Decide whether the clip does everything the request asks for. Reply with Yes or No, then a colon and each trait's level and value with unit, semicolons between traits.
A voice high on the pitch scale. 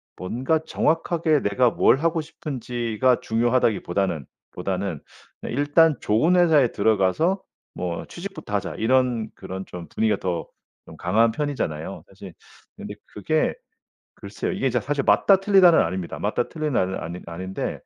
No: low, 115 Hz